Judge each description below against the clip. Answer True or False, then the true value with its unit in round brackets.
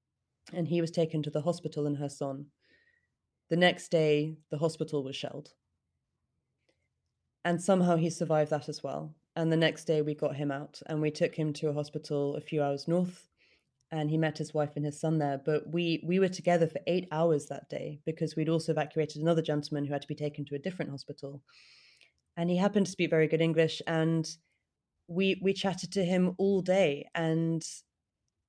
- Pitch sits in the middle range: True (155 Hz)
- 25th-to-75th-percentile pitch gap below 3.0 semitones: True (2.5 semitones)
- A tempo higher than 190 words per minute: True (200 wpm)